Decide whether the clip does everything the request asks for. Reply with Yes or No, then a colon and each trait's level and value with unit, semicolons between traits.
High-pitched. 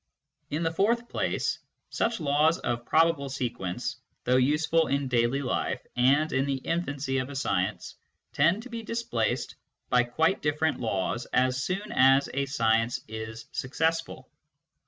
No: medium, 140 Hz